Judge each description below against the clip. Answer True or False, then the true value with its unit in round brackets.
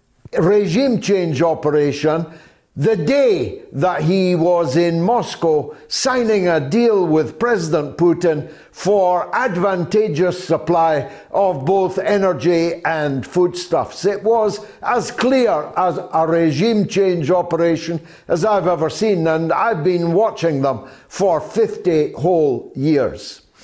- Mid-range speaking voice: True (175 Hz)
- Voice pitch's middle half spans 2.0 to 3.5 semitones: False (3.9 semitones)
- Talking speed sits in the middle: False (115 wpm)